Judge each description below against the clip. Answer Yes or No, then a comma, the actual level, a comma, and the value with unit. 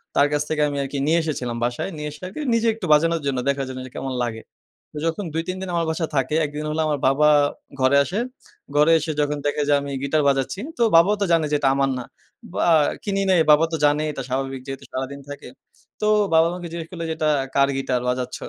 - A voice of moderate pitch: Yes, medium, 150 Hz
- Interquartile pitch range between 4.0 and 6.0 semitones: No, average, 3.4 semitones